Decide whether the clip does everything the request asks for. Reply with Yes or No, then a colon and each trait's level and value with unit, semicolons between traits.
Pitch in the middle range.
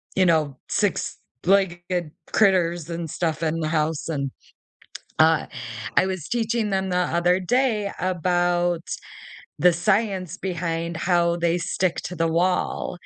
Yes: medium, 175 Hz